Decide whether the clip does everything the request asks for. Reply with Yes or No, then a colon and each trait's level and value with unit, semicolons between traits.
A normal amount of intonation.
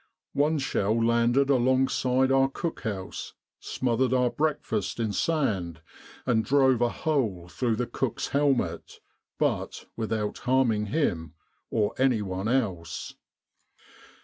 Yes: average, 4.0 semitones